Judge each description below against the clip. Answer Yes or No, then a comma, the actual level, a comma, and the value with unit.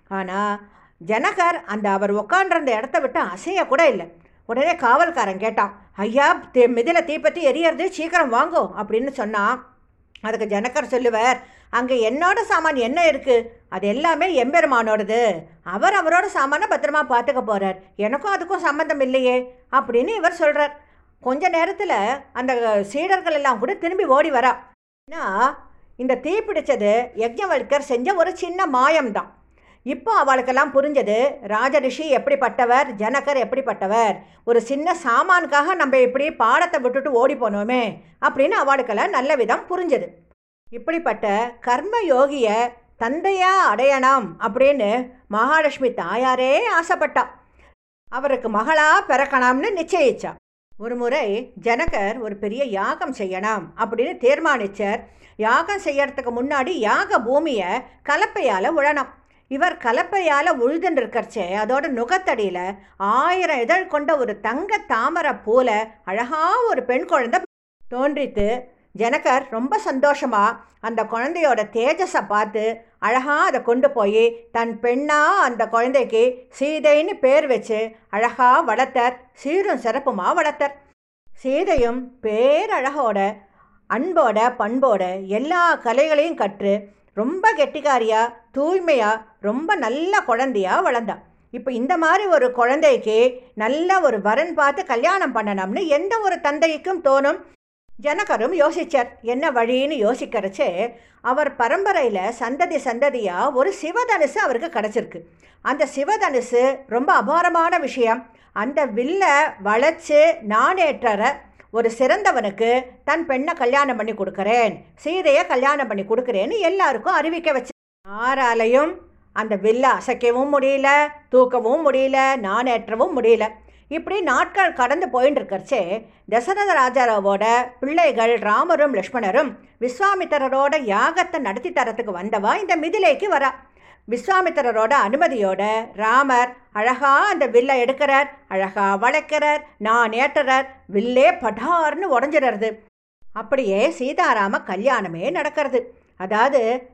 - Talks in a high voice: Yes, very high, 265 Hz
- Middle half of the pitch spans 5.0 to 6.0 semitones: Yes, average, 5.3 semitones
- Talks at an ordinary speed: No, slow, 110 wpm